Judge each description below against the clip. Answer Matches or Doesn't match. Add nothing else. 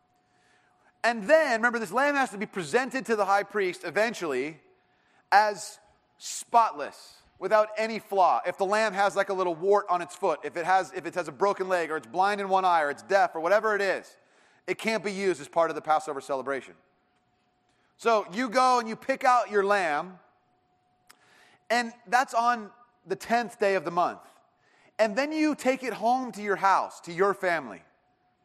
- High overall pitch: Matches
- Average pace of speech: Matches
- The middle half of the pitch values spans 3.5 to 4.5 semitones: Matches